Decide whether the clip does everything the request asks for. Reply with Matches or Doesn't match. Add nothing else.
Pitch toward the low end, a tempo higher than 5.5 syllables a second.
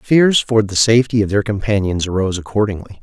Matches